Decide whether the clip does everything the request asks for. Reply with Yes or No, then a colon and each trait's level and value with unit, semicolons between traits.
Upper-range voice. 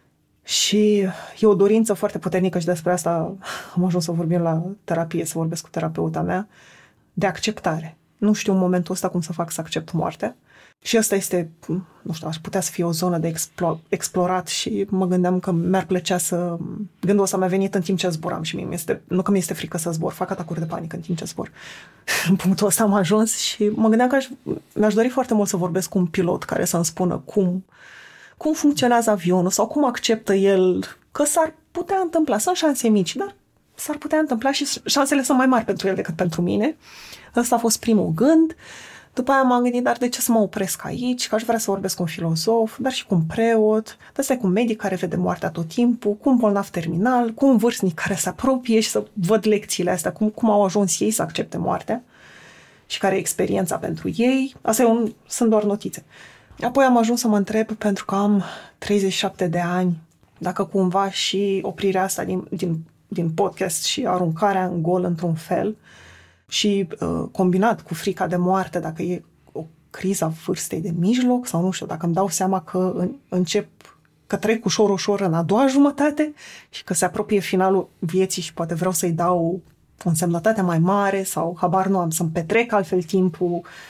Yes: high, 195 Hz